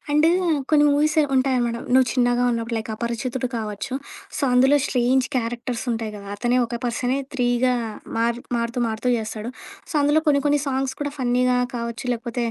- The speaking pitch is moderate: No, high, 245 Hz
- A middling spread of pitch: No, narrow, 2.1 semitones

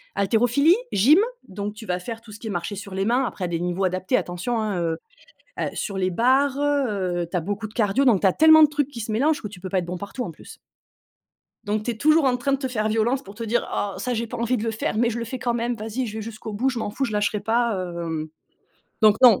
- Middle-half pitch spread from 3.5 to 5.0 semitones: Yes, average, 4.1 semitones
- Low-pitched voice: No, high, 220 Hz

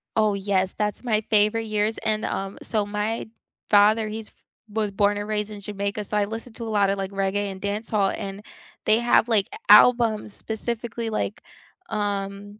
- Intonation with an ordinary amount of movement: No, narrow, 1.5 semitones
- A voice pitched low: No, high, 210 Hz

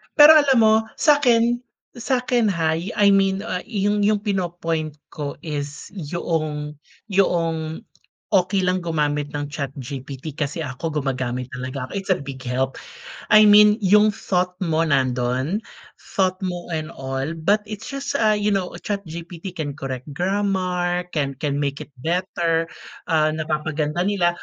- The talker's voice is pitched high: No, medium, 170 Hz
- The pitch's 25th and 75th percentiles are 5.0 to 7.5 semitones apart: Yes, average, 5.3 semitones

